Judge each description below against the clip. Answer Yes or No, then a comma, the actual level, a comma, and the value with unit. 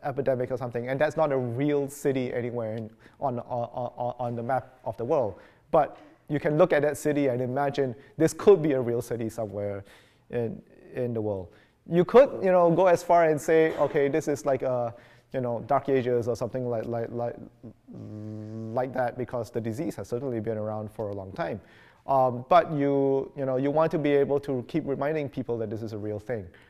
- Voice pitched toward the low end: Yes, low, 130 Hz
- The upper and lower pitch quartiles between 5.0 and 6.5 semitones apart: No, average, 3.4 semitones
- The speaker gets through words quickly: Yes, fast, 215 wpm